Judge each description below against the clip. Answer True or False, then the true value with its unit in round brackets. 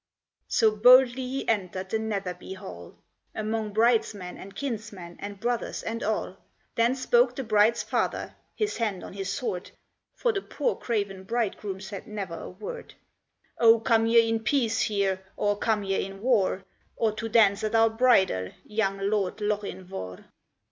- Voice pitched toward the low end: False (215 Hz)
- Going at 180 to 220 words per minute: False (155 wpm)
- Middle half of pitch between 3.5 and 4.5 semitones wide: False (2.9 semitones)